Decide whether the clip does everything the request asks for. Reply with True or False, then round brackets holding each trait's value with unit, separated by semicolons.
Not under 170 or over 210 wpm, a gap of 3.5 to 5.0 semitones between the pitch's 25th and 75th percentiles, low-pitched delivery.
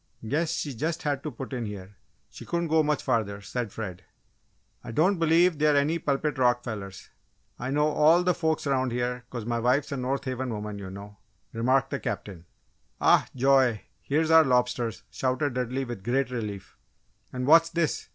True (180 wpm; 4.5 semitones; 130 Hz)